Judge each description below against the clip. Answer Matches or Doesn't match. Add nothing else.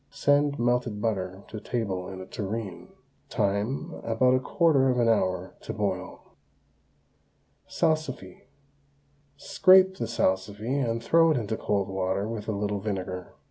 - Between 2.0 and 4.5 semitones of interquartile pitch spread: Doesn't match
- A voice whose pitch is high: Doesn't match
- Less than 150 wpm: Matches